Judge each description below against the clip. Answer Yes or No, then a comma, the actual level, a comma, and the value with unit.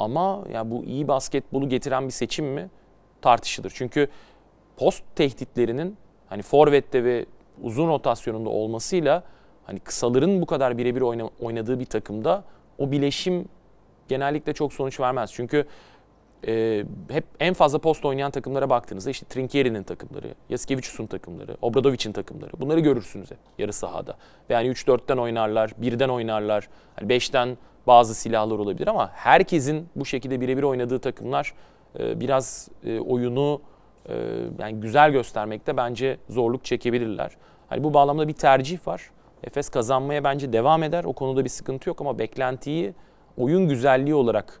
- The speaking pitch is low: Yes, low, 130 Hz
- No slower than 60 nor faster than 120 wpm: No, average, 135 wpm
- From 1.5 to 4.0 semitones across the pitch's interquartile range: Yes, average, 3.3 semitones